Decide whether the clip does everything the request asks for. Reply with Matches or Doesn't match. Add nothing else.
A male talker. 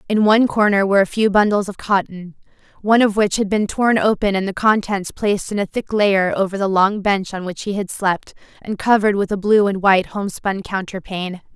Doesn't match